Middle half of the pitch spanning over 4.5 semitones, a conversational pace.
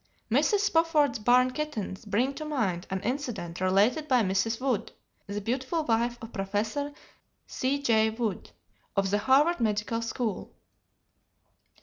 No: average, 5.0 semitones; slow, 125 wpm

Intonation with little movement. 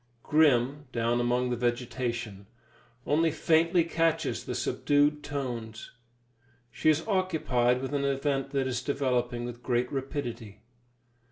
No: average, 3.4 semitones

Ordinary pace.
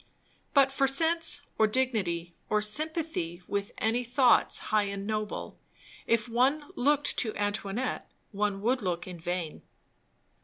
No: slow, 130 wpm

